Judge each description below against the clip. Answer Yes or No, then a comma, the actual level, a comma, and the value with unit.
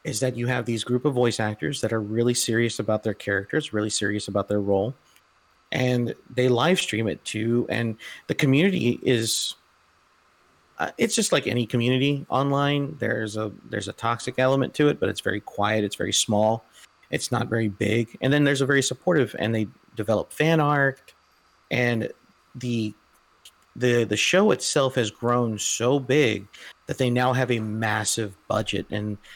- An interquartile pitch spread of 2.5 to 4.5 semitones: Yes, average, 3.3 semitones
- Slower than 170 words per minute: No, average, 175 wpm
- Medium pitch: No, low, 120 Hz